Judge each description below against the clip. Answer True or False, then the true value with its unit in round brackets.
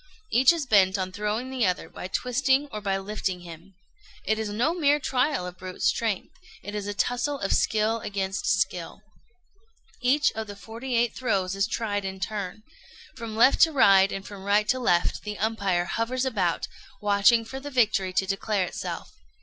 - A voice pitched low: False (210 Hz)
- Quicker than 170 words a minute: True (180 wpm)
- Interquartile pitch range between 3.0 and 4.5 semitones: True (4.2 semitones)